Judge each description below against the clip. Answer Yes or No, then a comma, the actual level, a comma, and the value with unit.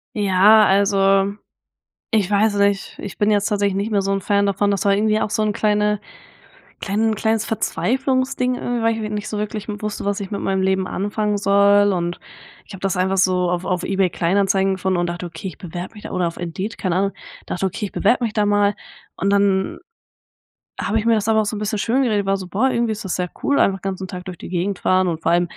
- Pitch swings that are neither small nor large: No, narrow, 2.0 semitones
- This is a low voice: No, high, 200 Hz